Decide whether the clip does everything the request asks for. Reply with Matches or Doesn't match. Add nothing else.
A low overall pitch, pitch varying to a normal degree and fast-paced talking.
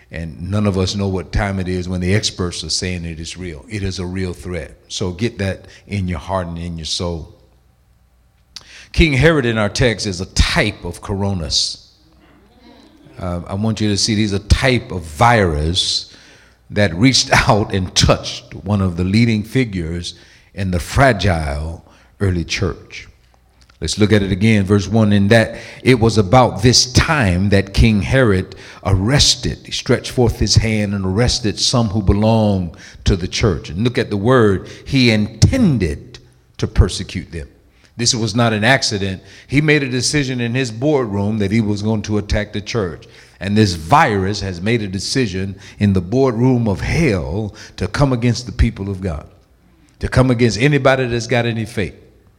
Doesn't match